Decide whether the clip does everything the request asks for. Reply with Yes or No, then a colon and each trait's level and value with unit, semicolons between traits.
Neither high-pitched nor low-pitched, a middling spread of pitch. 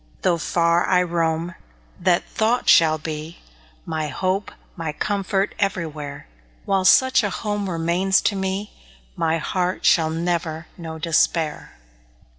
Yes: medium, 175 Hz; average, 3.0 semitones